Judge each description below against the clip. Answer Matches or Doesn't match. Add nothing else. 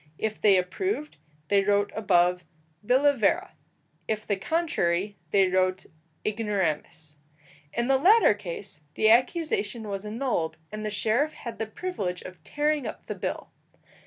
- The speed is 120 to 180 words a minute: Matches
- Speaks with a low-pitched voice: Doesn't match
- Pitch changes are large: Matches